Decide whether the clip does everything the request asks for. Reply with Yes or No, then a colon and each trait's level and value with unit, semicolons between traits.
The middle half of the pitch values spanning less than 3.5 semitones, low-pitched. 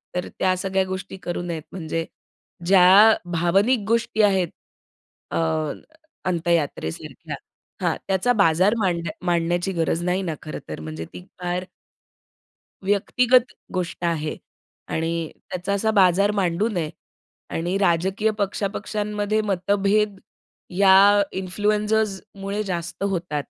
No: average, 3.1 semitones; high, 190 Hz